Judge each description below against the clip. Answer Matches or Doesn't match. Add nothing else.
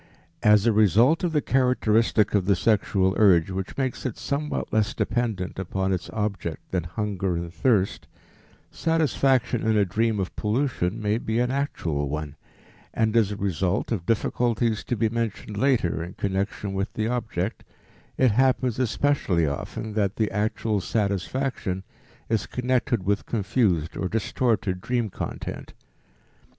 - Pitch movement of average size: Matches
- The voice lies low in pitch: Matches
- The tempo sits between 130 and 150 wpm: Matches